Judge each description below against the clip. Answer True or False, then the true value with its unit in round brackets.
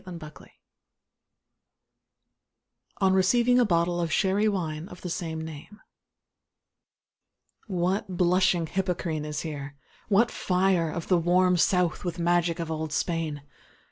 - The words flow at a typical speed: False (125 wpm)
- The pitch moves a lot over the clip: False (2.7 semitones)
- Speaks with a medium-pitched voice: True (175 Hz)